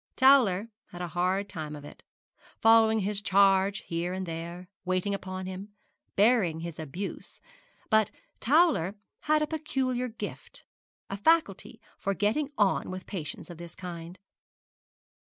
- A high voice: Yes, high, 195 Hz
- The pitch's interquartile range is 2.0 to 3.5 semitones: No, average, 4.1 semitones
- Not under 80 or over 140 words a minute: Yes, slow, 135 wpm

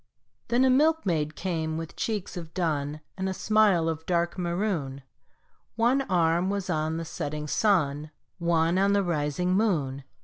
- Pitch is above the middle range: No, medium, 170 Hz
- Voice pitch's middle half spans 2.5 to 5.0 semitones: Yes, average, 4.2 semitones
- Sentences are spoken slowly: No, average, 150 wpm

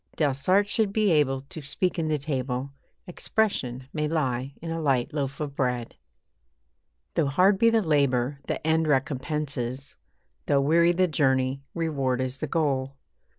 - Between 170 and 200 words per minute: No, average, 150 wpm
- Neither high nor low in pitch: Yes, medium, 145 Hz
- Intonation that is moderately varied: Yes, average, 3.7 semitones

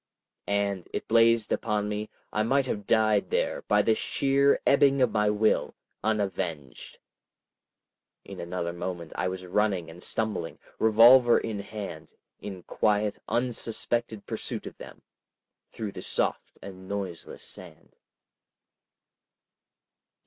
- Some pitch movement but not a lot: Yes, average, 3.3 semitones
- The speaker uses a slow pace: Yes, slow, 120 wpm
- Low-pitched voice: Yes, low, 105 Hz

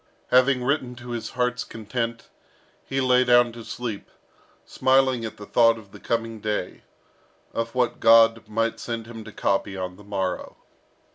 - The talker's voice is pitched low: Yes, low, 115 Hz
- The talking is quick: No, average, 160 wpm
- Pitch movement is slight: Yes, narrow, 2.1 semitones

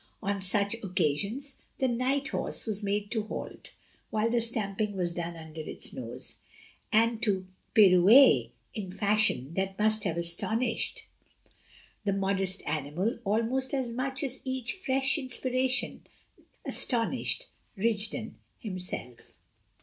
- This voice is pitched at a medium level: No, high, 215 Hz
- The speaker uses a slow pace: Yes, slow, 120 wpm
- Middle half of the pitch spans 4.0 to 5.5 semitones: Yes, average, 4.5 semitones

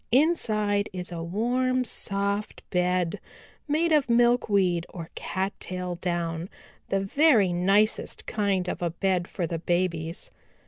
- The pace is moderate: No, slow, 125 wpm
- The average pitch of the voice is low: No, high, 195 Hz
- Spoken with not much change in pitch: No, average, 3.8 semitones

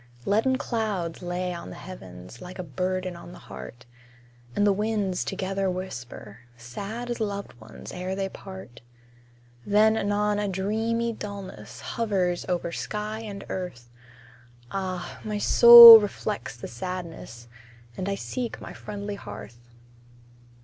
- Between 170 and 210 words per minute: No, slow, 135 wpm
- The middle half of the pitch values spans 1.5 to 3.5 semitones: Yes, average, 3.1 semitones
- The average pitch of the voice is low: No, high, 190 Hz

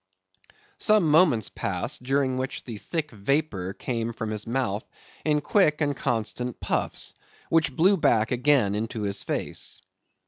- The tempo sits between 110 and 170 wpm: Yes, average, 140 wpm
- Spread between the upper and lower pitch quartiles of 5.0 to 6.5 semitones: Yes, average, 5.3 semitones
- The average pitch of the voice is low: Yes, low, 125 Hz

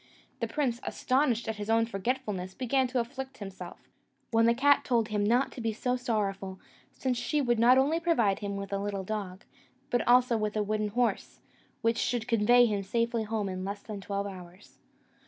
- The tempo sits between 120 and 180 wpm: No, average, 195 wpm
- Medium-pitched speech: No, high, 225 Hz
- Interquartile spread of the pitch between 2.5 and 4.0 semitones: Yes, average, 3.5 semitones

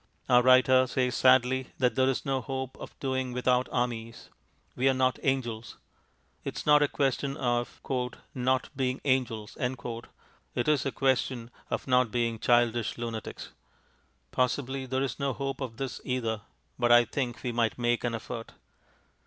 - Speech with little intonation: Yes, narrow, 1.6 semitones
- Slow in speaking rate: No, average, 160 wpm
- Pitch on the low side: Yes, low, 125 Hz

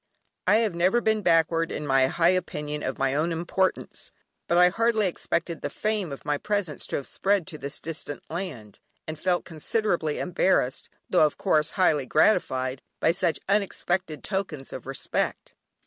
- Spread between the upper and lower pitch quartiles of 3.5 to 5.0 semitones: Yes, average, 4.1 semitones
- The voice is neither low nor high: Yes, medium, 170 Hz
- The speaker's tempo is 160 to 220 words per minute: Yes, average, 165 wpm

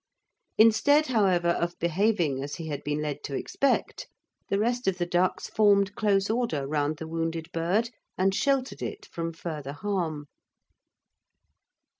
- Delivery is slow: No, average, 145 wpm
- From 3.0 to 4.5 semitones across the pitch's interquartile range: No, average, 5.1 semitones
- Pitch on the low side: No, medium, 175 Hz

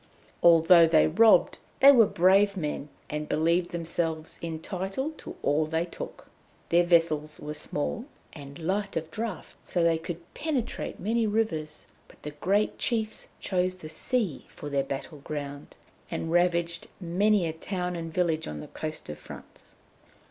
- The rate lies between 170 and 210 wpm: No, average, 155 wpm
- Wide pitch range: No, average, 3.7 semitones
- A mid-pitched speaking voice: Yes, medium, 170 Hz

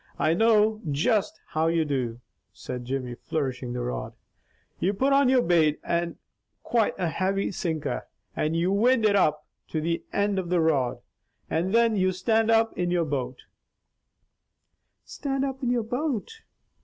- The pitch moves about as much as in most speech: No, wide, 6.5 semitones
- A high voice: No, medium, 180 Hz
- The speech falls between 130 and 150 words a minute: No, average, 165 wpm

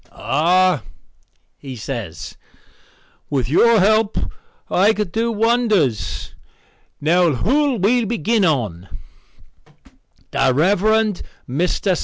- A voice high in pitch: No, medium, 180 Hz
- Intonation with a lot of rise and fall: Yes, wide, 8.3 semitones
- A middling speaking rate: No, slow, 90 wpm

